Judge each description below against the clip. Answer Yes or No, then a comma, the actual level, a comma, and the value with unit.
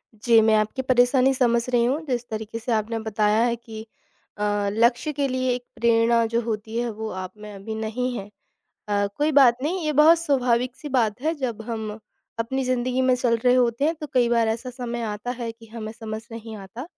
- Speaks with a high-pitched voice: Yes, high, 235 Hz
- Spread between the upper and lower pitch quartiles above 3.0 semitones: No, narrow, 2.5 semitones